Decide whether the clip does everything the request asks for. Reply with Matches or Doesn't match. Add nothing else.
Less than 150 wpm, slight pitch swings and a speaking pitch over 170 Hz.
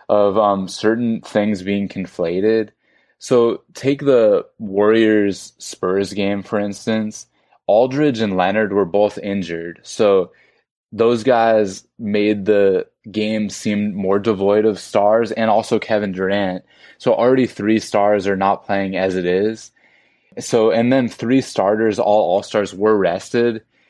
Doesn't match